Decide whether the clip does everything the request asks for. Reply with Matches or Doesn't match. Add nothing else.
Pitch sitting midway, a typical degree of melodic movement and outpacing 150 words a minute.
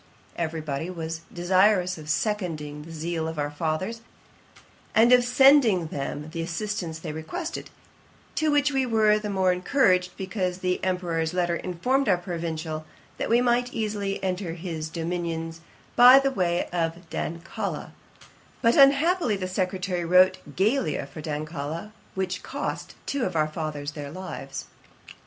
Doesn't match